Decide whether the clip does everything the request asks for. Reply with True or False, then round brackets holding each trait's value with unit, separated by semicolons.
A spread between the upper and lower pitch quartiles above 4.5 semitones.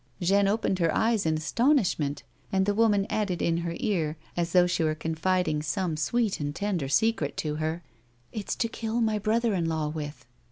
True (5.1 semitones)